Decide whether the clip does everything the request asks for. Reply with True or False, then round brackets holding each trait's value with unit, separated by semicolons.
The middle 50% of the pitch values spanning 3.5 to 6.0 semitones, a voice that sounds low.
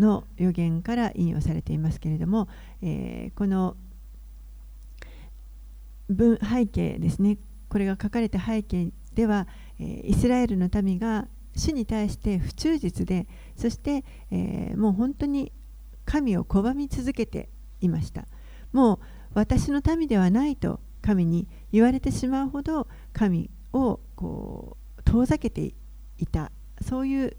False (5.3 semitones; 210 Hz)